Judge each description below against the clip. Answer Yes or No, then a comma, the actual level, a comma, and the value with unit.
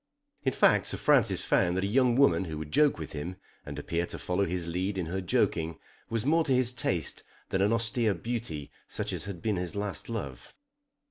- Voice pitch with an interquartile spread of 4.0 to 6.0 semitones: Yes, wide, 5.4 semitones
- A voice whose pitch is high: No, very low, 95 Hz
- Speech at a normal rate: No, fast, 210 wpm